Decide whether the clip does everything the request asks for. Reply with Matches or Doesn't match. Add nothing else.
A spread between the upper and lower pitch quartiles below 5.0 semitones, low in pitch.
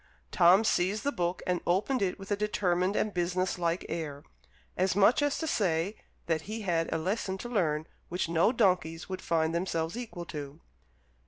Doesn't match